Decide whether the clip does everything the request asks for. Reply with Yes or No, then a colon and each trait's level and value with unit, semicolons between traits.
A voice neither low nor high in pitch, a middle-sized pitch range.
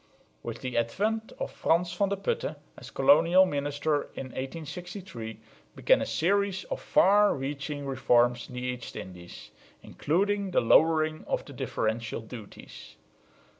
No: medium, 150 Hz; wide, 7.2 semitones